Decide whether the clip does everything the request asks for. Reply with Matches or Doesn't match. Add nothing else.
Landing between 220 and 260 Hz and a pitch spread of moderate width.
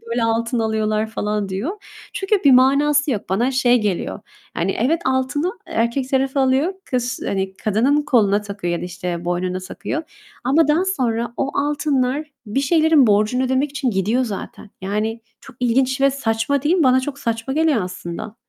Matches